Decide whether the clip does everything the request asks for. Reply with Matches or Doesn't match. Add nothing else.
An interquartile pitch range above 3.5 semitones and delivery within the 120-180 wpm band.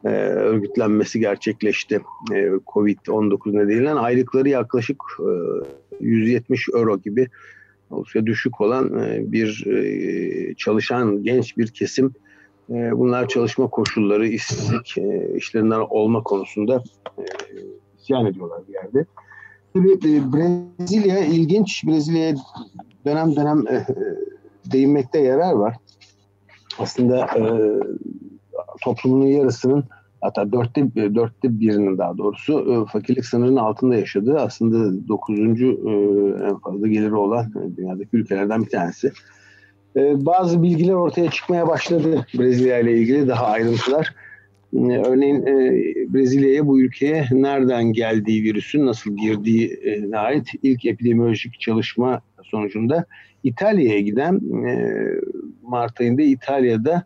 Doesn't match